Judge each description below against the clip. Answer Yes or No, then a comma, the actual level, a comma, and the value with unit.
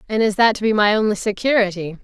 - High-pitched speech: Yes, high, 210 Hz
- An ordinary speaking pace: No, fast, 235 wpm